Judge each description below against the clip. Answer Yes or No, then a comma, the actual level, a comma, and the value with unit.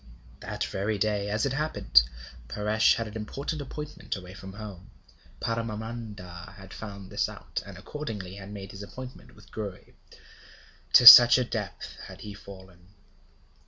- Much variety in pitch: No, average, 2.9 semitones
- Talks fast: No, average, 150 wpm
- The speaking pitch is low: Yes, low, 105 Hz